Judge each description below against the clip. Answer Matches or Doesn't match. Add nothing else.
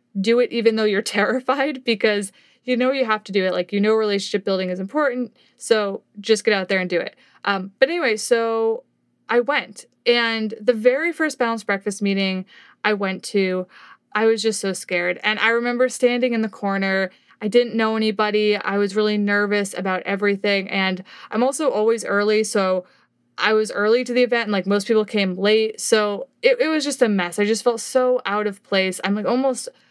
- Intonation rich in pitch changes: Doesn't match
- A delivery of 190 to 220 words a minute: Matches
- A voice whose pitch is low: Doesn't match